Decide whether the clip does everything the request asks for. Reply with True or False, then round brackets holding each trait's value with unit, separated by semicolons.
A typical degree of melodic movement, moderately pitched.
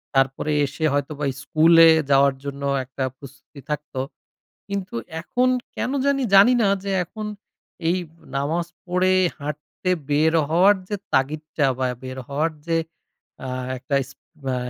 True (4.6 semitones; 150 Hz)